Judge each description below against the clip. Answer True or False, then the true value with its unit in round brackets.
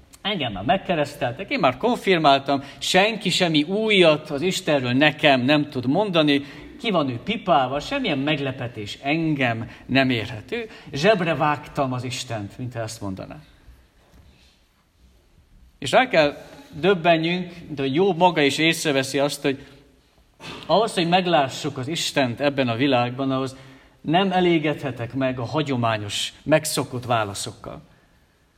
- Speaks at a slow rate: False (120 wpm)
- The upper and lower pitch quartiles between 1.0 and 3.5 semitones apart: False (4.5 semitones)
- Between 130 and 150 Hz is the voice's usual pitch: True (140 Hz)